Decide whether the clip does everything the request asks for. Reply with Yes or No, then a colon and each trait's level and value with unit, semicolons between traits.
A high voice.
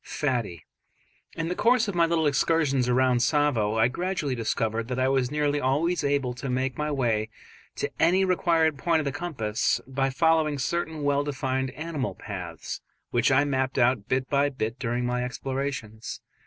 No: low, 135 Hz